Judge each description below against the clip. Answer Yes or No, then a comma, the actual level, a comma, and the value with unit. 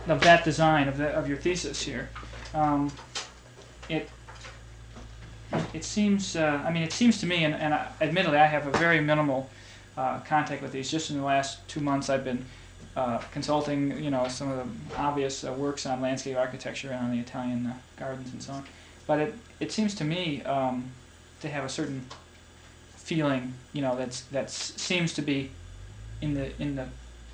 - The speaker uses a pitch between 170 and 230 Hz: No, low, 135 Hz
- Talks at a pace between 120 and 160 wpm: No, average, 190 wpm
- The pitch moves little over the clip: No, average, 3.4 semitones